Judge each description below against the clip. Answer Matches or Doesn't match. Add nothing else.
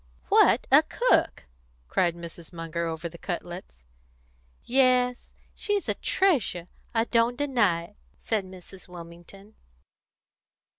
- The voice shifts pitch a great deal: Matches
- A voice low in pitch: Doesn't match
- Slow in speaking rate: Matches